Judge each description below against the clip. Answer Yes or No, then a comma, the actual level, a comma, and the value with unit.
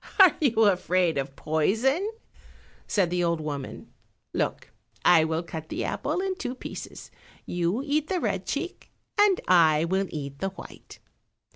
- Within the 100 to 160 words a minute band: Yes, average, 150 wpm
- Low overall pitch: No, medium, 185 Hz